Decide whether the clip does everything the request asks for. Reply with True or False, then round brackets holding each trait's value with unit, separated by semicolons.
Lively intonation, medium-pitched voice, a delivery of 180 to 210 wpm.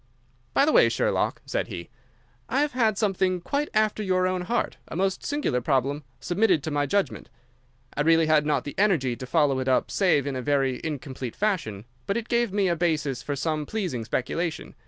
True (6.1 semitones; 165 Hz; 190 wpm)